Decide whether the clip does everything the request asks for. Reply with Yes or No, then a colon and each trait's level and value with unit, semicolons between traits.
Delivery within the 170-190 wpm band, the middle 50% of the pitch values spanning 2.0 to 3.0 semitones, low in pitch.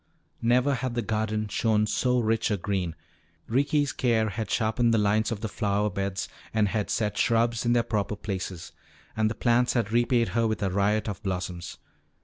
Yes: average, 185 wpm; narrow, 2.5 semitones; low, 110 Hz